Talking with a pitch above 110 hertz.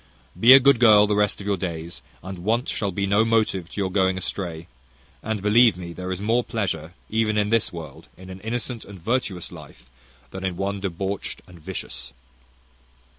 No: low, 100 Hz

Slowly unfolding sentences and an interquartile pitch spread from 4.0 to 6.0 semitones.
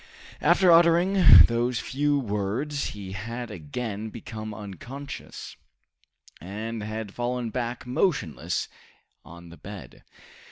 Yes: slow, 105 wpm; average, 4.8 semitones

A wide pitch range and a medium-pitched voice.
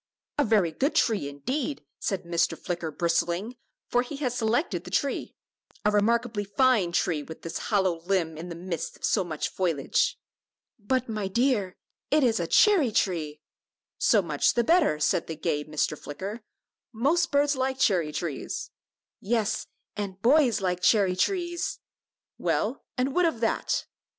No: wide, 6.8 semitones; high, 205 Hz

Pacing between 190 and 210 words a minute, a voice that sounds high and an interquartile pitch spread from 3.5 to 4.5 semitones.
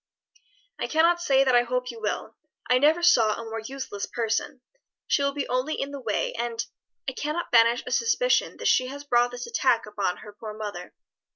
Yes: average, 200 wpm; very high, 250 Hz; average, 3.9 semitones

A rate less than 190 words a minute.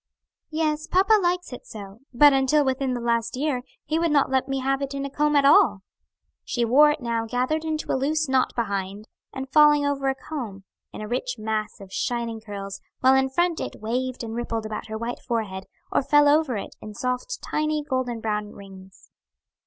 No: average, 200 wpm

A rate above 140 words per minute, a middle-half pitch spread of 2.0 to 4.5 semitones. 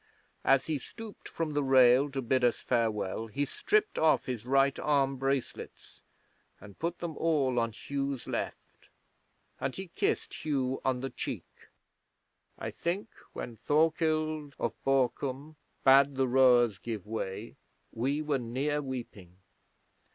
No: slow, 135 wpm; average, 3.4 semitones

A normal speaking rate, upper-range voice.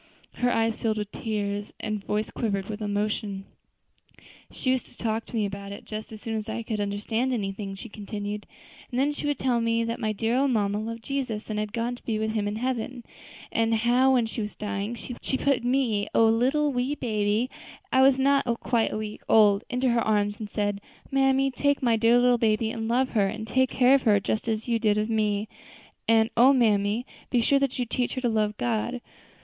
No: fast, 220 wpm; high, 225 Hz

